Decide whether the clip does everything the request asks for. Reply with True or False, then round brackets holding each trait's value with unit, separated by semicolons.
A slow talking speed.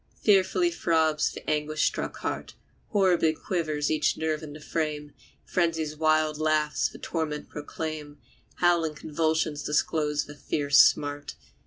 True (130 wpm)